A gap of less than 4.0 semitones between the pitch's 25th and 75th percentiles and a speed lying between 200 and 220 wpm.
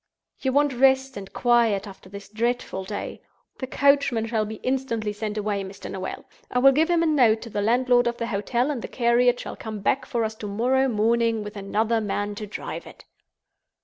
Yes: average, 3.6 semitones; fast, 205 wpm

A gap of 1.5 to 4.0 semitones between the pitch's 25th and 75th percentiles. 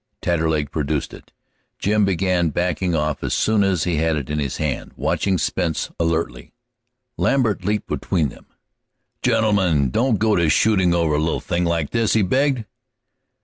No: average, 4.8 semitones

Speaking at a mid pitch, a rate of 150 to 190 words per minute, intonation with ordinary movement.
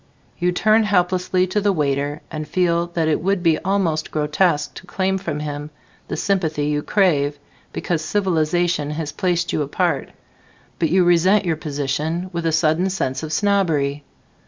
Yes: medium, 170 Hz; average, 160 wpm; average, 3.5 semitones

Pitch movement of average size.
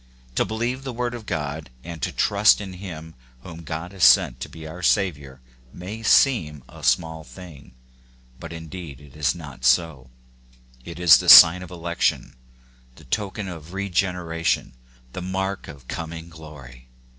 Yes: average, 3.6 semitones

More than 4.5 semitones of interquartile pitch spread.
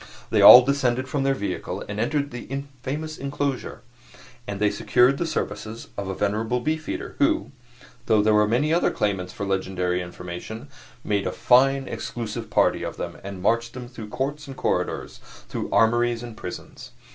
Yes: average, 4.9 semitones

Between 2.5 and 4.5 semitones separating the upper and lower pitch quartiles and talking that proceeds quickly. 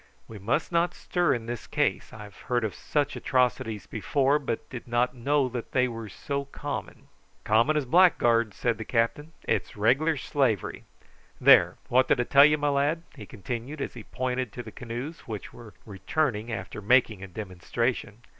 No: average, 3.9 semitones; average, 175 wpm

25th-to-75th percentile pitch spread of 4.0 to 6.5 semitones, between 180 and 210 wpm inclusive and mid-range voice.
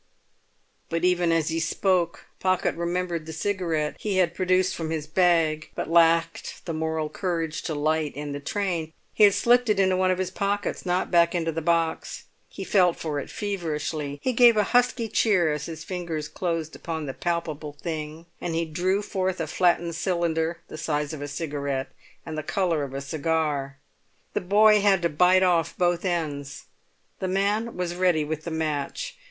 No: average, 3.0 semitones; average, 185 wpm; medium, 170 Hz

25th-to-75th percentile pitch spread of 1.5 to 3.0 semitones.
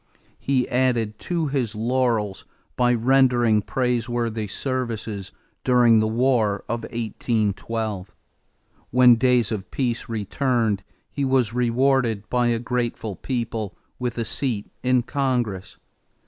Yes: narrow, 2.6 semitones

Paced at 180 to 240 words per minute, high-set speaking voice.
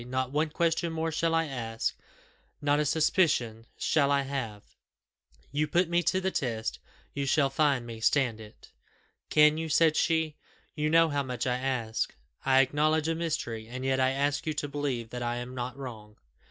No: average, 185 wpm; medium, 140 Hz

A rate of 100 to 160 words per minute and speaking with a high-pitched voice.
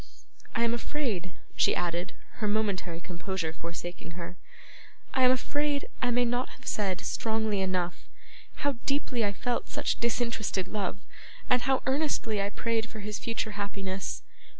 Yes: average, 150 wpm; high, 215 Hz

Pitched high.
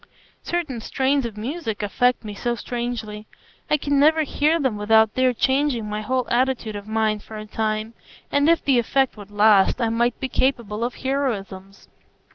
Yes: high, 235 Hz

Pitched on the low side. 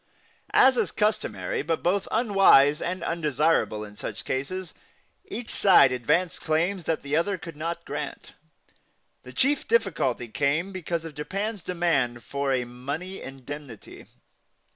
No: medium, 165 Hz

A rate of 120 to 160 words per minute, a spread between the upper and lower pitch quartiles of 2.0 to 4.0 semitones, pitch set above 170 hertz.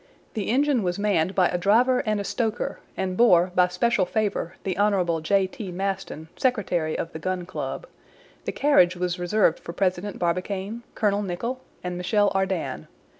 No: average, 170 wpm; average, 2.9 semitones; high, 190 Hz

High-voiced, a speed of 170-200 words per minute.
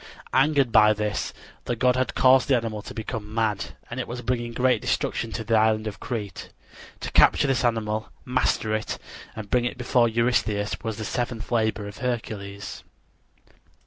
No: low, 115 Hz; average, 175 wpm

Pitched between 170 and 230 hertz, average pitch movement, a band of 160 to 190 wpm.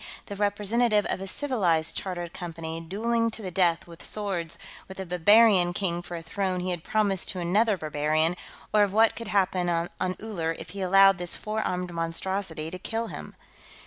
Yes: medium, 185 Hz; average, 3.3 semitones; average, 185 wpm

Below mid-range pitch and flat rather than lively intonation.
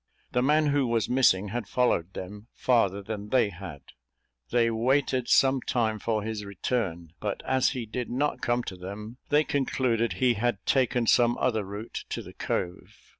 No: low, 115 Hz; average, 3.8 semitones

